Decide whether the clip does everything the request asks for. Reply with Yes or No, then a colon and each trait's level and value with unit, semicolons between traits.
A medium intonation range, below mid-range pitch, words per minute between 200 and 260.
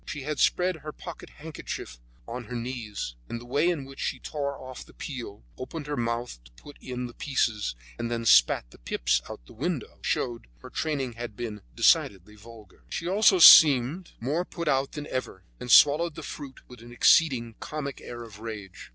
Yes: average, 4.4 semitones; low, 125 Hz; fast, 205 wpm